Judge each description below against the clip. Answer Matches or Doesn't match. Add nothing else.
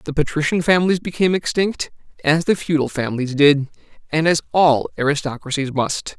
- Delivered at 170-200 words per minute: Doesn't match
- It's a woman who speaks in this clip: Doesn't match